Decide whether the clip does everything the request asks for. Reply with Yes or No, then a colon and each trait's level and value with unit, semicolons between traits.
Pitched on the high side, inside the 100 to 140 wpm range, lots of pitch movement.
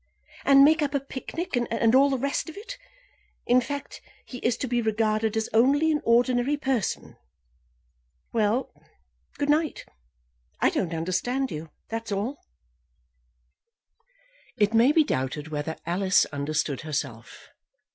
Yes: high, 235 Hz; slow, 135 wpm; wide, 6.1 semitones